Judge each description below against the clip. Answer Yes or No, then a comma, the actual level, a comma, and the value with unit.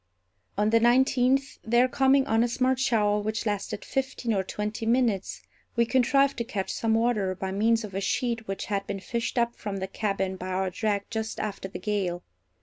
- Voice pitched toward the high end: Yes, high, 220 Hz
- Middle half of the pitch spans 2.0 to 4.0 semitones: Yes, average, 3.4 semitones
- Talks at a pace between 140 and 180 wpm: No, average, 195 wpm